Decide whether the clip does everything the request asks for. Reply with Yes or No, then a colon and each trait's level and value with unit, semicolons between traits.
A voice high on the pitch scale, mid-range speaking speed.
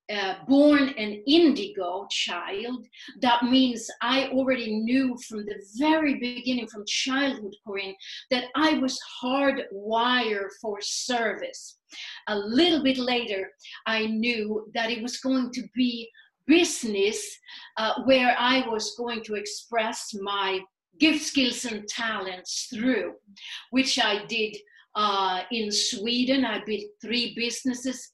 No: high, 240 Hz; slow, 125 wpm